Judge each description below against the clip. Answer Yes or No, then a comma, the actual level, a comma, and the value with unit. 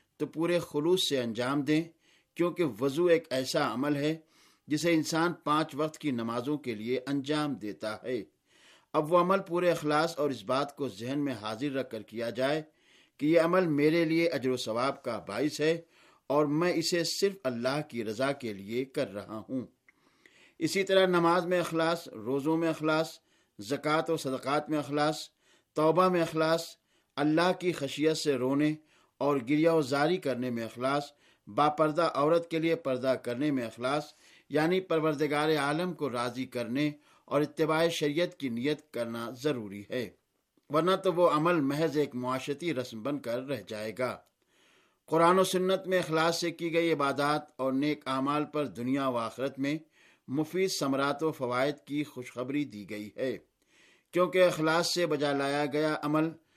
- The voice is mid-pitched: Yes, medium, 150 Hz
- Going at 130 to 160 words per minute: No, average, 170 wpm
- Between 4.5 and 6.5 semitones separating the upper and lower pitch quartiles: No, average, 3.7 semitones